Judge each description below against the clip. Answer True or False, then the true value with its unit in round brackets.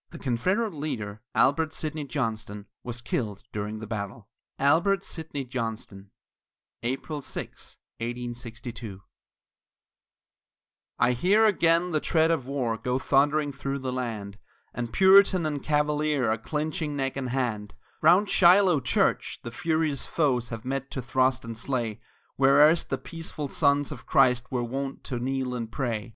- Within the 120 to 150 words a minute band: True (145 wpm)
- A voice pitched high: False (135 Hz)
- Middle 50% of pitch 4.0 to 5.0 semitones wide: True (4.5 semitones)